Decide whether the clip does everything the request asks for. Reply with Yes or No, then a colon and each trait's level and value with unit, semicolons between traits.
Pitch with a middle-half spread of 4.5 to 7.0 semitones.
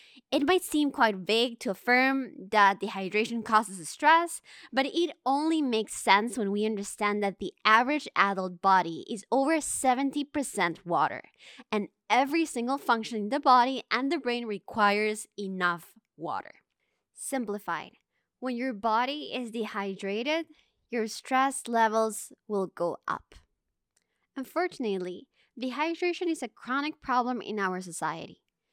Yes: average, 4.9 semitones